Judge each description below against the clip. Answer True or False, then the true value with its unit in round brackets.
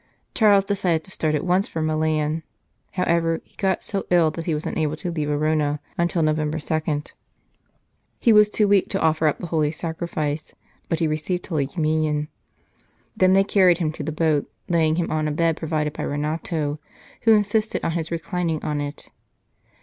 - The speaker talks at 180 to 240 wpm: True (185 wpm)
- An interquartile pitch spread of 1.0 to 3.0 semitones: True (2.6 semitones)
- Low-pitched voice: False (160 Hz)